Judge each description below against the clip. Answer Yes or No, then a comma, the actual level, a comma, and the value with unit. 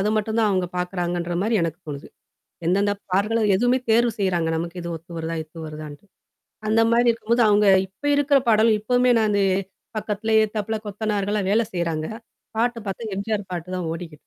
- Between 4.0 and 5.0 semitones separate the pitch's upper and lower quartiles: Yes, average, 4.3 semitones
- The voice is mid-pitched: No, high, 205 Hz